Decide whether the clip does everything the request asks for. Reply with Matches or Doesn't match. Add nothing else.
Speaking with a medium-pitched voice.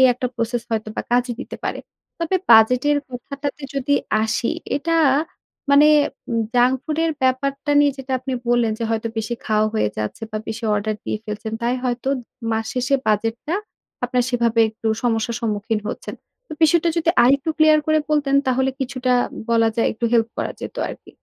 Doesn't match